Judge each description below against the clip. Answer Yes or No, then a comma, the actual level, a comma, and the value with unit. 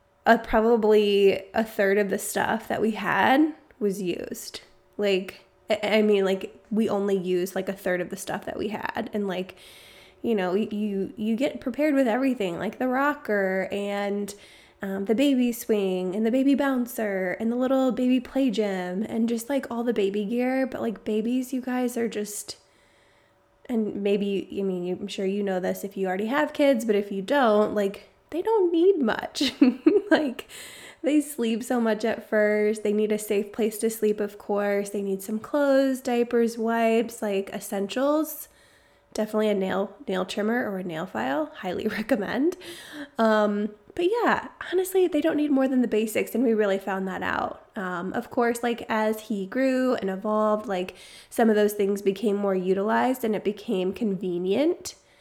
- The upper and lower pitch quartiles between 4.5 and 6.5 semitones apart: No, average, 4.1 semitones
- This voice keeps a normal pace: Yes, average, 180 wpm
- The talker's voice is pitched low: No, high, 215 Hz